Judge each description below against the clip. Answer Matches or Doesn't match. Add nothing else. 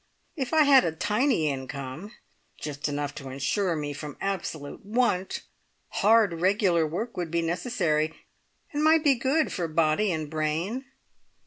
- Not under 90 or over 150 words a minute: Matches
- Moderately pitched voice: Matches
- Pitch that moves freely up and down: Matches